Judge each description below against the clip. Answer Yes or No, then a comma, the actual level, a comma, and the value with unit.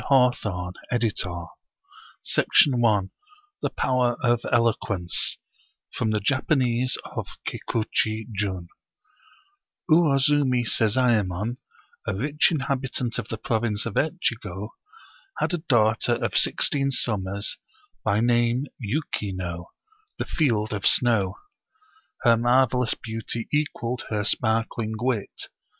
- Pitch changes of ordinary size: Yes, average, 3.5 semitones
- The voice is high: No, low, 115 Hz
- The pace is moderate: No, slow, 110 wpm